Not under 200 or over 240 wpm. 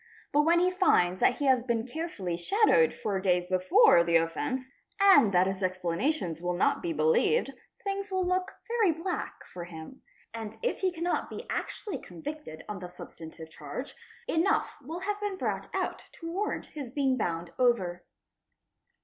No: average, 165 wpm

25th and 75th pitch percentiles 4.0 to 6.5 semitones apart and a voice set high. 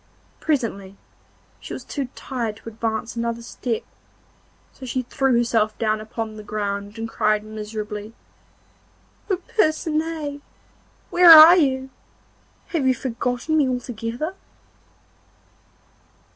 Yes: average, 4.7 semitones; high, 235 Hz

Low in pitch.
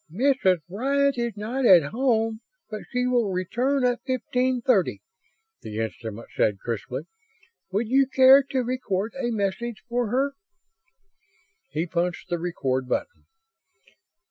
No: high, 230 Hz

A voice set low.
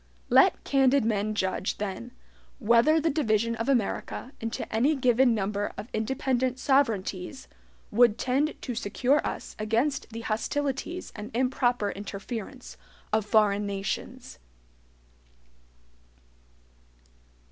No: high, 230 Hz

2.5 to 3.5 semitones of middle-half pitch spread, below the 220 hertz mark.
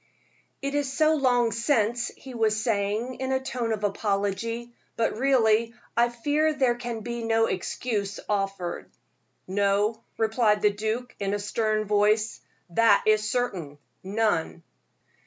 No: average, 2.8 semitones; high, 225 Hz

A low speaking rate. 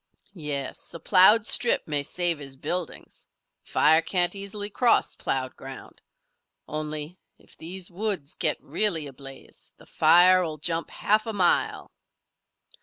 Yes: slow, 130 wpm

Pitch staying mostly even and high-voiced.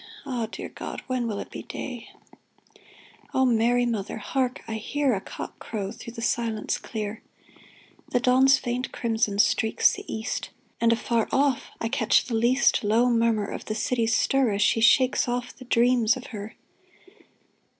Yes: narrow, 2.3 semitones; high, 235 Hz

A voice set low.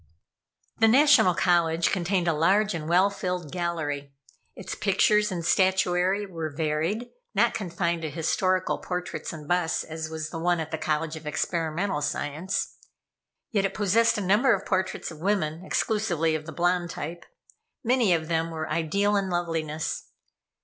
No: medium, 175 Hz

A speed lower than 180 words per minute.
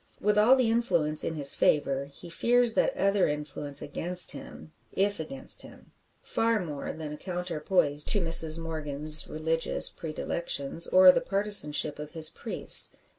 Yes: average, 150 wpm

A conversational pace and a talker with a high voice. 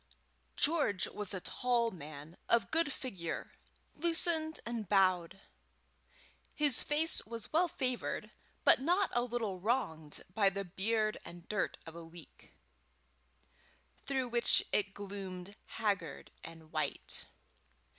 No: slow, 120 wpm; high, 210 Hz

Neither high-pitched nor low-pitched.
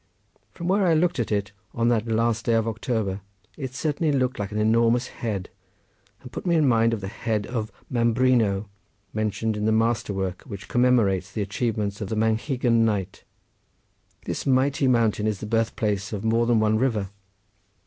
No: low, 115 Hz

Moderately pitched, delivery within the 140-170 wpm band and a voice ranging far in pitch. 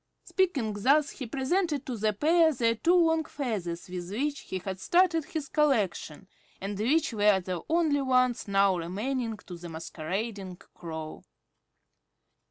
No: high, 230 Hz; average, 150 wpm; wide, 7.6 semitones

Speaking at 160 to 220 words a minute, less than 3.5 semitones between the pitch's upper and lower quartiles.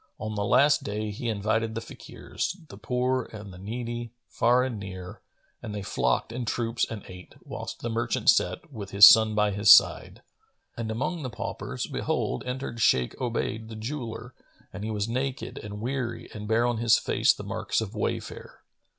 Yes: average, 185 wpm; narrow, 2.6 semitones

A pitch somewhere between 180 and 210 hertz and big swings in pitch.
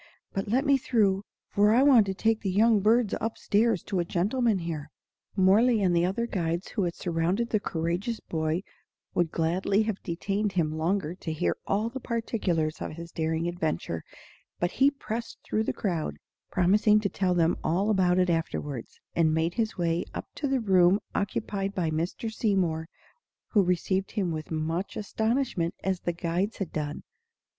No: high, 190 Hz; average, 4.3 semitones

